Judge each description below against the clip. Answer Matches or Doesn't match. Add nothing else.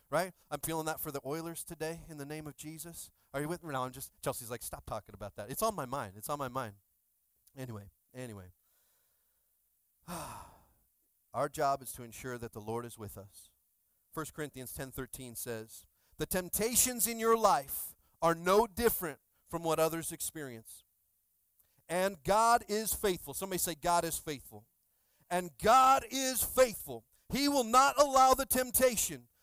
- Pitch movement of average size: Doesn't match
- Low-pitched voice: Doesn't match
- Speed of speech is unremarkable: Matches